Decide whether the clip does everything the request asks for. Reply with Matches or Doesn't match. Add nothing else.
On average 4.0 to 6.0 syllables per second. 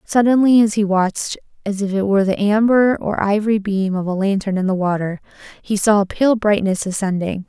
Matches